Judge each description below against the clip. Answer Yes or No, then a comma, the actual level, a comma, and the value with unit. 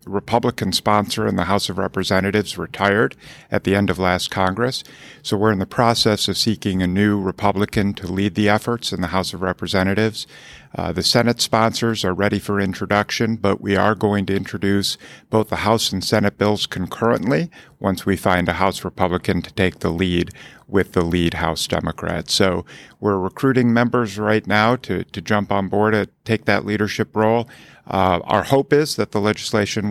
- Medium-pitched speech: No, low, 100 Hz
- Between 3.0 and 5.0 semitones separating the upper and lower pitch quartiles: No, narrow, 2.5 semitones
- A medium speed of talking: Yes, average, 185 wpm